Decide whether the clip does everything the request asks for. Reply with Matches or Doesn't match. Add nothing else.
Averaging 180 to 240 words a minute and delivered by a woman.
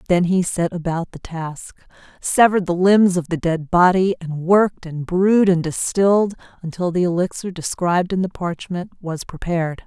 Doesn't match